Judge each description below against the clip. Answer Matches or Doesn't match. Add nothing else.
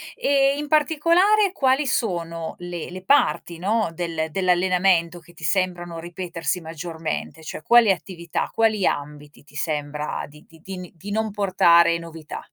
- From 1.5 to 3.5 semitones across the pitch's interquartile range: Doesn't match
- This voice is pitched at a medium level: Matches